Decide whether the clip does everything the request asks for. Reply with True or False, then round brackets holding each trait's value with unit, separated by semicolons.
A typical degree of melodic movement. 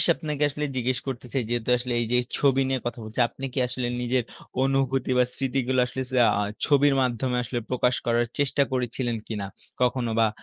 False (1.8 semitones)